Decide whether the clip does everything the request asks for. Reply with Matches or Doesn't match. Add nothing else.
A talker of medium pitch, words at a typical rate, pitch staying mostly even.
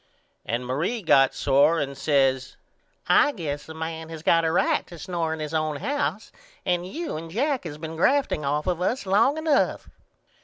Doesn't match